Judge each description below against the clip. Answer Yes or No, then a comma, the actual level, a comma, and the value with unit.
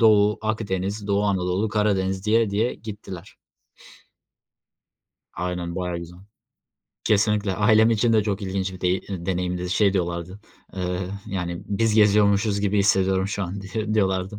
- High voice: No, low, 100 Hz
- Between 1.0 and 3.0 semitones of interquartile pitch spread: Yes, narrow, 2.4 semitones